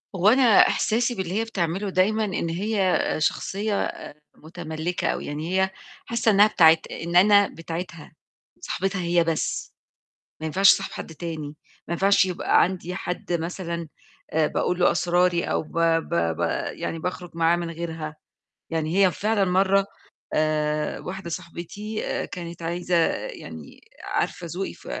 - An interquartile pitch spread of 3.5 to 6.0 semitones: No, average, 2.9 semitones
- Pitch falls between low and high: Yes, medium, 175 Hz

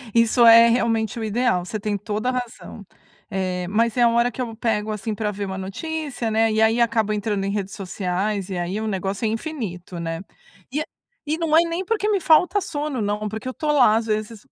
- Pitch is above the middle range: Yes, high, 220 Hz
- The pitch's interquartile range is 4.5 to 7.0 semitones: No, average, 3.6 semitones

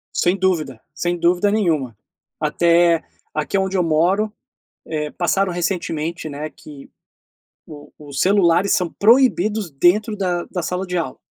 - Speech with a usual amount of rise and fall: Yes, average, 3.5 semitones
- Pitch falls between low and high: Yes, medium, 175 Hz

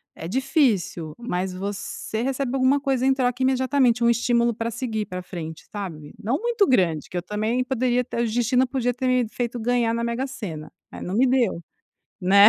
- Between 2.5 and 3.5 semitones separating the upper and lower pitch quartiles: No, average, 4.3 semitones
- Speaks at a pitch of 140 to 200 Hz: No, high, 235 Hz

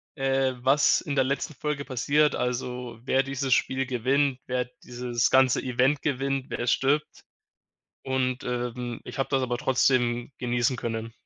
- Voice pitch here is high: No, low, 130 Hz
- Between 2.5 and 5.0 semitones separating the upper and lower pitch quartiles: No, narrow, 1.8 semitones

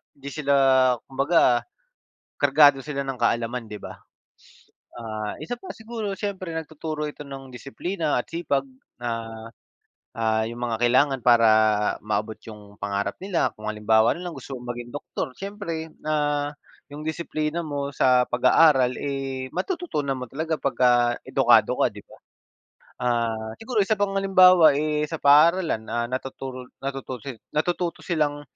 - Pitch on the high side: No, medium, 140 Hz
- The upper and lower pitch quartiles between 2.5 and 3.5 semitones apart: No, average, 4.8 semitones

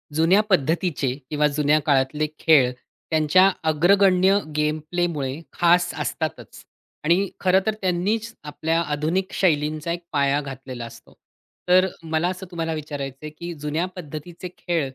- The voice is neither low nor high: Yes, medium, 160 Hz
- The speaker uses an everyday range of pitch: Yes, average, 3.3 semitones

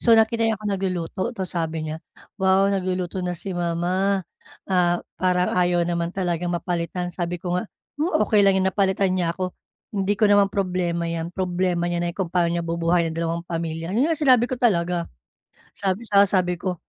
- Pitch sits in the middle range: Yes, medium, 180 Hz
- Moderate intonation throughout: No, narrow, 2.2 semitones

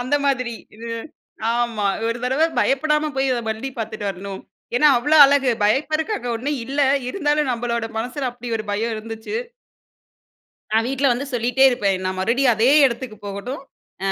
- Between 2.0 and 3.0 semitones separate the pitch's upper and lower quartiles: No, average, 3.5 semitones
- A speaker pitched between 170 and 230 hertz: No, high, 245 Hz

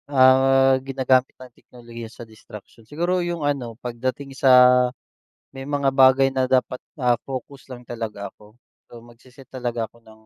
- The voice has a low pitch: Yes, low, 130 Hz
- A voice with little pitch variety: Yes, narrow, 2.1 semitones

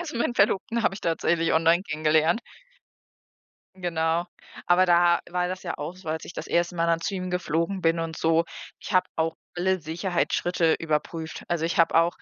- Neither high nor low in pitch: Yes, medium, 170 Hz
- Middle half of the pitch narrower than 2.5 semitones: Yes, narrow, 1.9 semitones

